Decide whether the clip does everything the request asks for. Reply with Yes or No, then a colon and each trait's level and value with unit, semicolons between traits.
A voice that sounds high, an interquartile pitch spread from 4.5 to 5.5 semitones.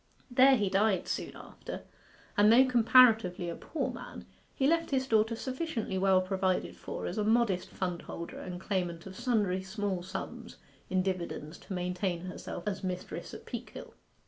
No: high, 195 Hz; average, 3.9 semitones